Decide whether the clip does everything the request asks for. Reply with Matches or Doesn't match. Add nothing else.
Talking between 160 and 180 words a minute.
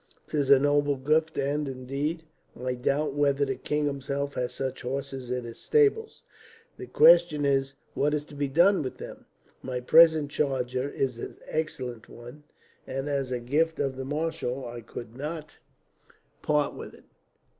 Matches